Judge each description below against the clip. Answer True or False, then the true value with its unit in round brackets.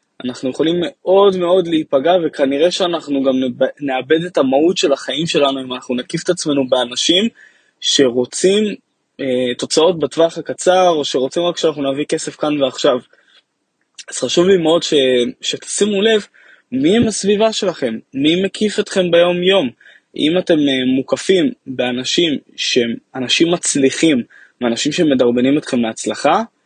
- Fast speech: False (135 wpm)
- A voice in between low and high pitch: True (160 Hz)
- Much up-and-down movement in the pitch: True (5.7 semitones)